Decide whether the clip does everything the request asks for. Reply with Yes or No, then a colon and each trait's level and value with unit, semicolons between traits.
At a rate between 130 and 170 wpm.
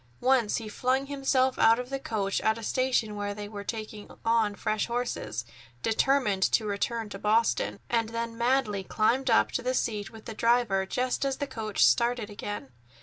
No: average, 185 wpm